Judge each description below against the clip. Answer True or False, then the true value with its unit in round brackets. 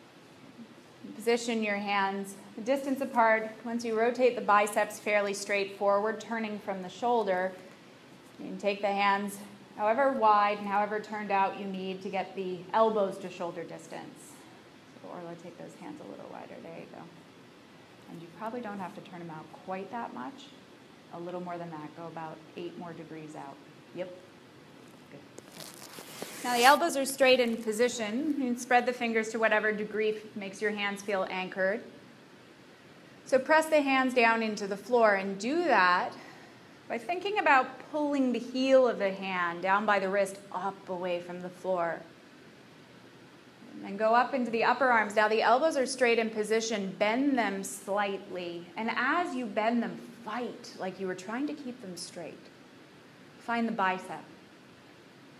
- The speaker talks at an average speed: True (170 wpm)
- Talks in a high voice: True (210 Hz)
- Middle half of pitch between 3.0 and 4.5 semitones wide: True (4.0 semitones)